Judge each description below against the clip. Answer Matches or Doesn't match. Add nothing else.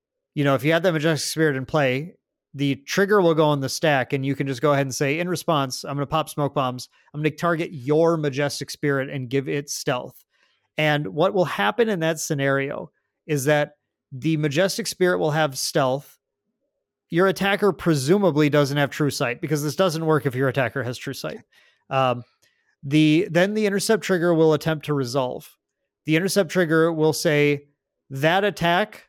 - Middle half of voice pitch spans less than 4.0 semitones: Matches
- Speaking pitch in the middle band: Matches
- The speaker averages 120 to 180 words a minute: Doesn't match